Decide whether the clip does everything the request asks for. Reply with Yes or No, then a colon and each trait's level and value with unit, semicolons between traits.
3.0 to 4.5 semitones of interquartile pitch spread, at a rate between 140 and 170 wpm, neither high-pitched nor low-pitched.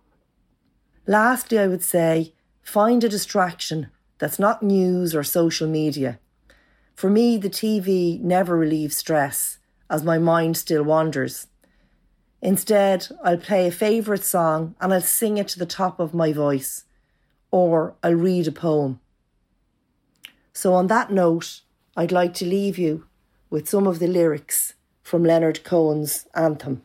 Yes: average, 3.5 semitones; average, 145 wpm; medium, 175 Hz